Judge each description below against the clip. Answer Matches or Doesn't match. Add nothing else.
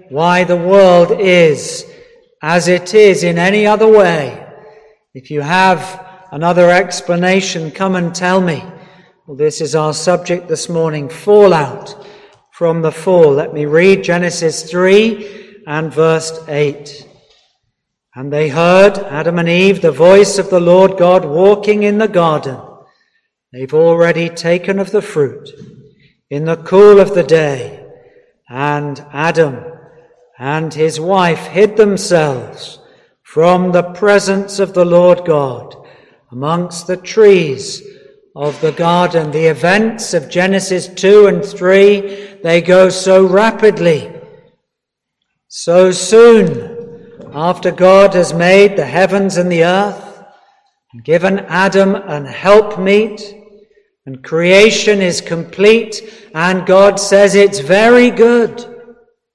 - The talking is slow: Matches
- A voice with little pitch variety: Doesn't match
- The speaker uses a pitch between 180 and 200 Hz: Matches